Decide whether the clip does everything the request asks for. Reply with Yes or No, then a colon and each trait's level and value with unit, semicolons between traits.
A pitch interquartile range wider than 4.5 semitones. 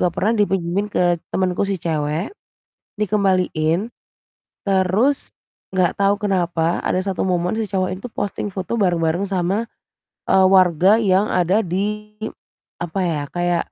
No: narrow, 2.5 semitones